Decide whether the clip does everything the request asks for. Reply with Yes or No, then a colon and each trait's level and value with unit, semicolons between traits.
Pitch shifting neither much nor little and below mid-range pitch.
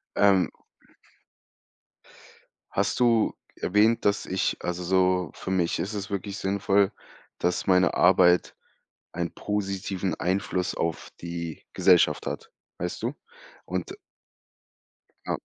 No: narrow, 2.3 semitones; very low, 95 Hz